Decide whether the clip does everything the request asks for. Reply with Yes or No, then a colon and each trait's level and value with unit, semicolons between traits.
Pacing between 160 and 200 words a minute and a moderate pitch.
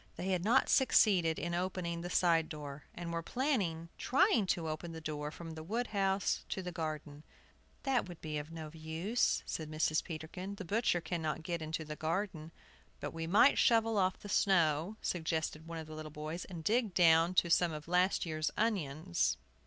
Yes: average, 190 wpm; medium, 170 Hz